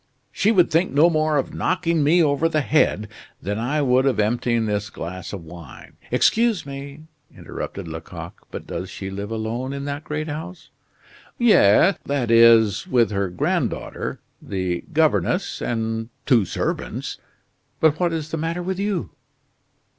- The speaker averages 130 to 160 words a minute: Yes, average, 155 wpm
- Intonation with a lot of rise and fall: Yes, wide, 7.2 semitones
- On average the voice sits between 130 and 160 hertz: Yes, medium, 140 Hz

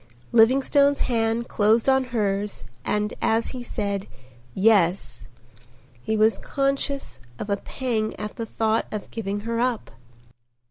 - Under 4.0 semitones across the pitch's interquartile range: Yes, average, 3.0 semitones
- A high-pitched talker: Yes, high, 225 Hz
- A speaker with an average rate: No, slow, 130 wpm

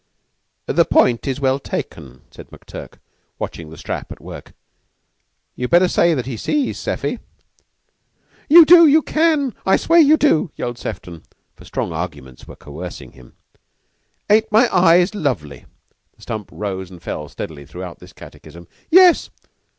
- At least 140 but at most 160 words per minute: Yes, average, 150 wpm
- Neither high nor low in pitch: No, low, 125 Hz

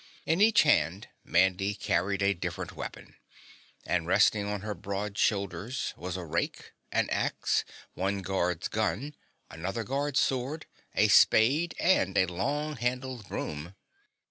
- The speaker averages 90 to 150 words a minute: Yes, slow, 135 wpm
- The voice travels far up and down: Yes, wide, 5.8 semitones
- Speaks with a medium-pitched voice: No, low, 100 Hz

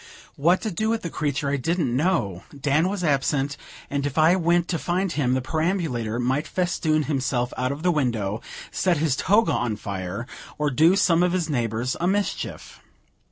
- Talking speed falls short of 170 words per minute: No, average, 185 wpm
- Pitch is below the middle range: No, medium, 150 Hz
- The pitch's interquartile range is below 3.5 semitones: No, wide, 5.5 semitones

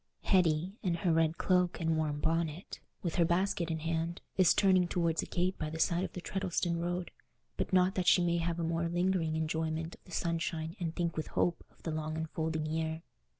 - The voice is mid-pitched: Yes, medium, 170 Hz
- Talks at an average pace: No, fast, 215 wpm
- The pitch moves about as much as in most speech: No, narrow, 1.8 semitones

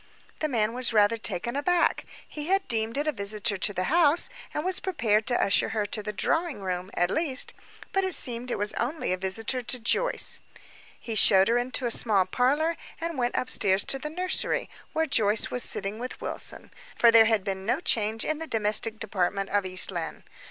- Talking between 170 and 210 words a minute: Yes, average, 200 wpm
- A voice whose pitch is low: No, high, 230 Hz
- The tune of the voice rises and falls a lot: Yes, wide, 6.0 semitones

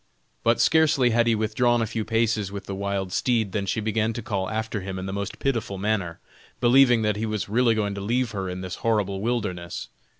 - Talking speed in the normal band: No, fast, 220 wpm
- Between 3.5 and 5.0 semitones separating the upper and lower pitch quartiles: No, average, 2.9 semitones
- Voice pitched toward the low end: Yes, low, 110 Hz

